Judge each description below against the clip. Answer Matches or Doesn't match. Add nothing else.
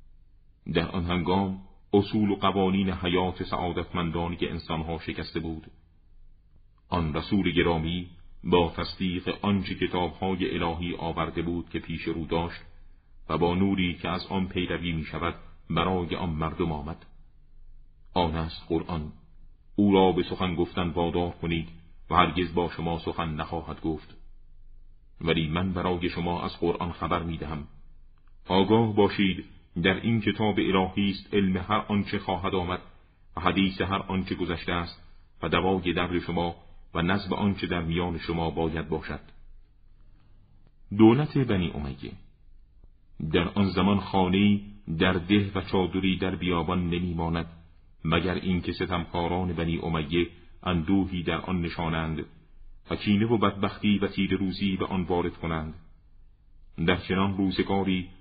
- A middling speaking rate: Matches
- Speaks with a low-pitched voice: Matches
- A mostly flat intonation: Matches